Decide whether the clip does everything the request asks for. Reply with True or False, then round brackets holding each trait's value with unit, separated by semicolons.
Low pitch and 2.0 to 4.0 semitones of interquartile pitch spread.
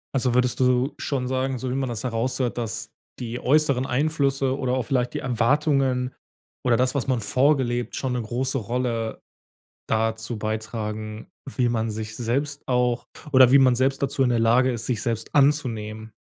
True (125 Hz; 2.5 semitones)